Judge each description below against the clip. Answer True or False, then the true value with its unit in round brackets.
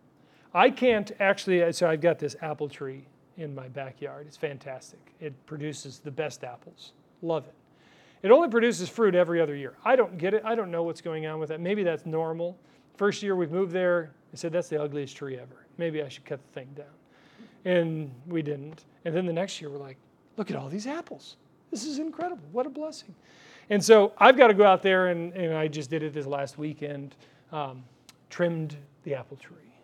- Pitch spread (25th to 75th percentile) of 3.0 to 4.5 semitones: False (4.9 semitones)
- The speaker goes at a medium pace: False (210 wpm)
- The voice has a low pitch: False (160 Hz)